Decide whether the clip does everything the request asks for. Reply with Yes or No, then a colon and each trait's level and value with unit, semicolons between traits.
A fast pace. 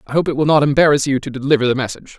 Yes: fast, 300 wpm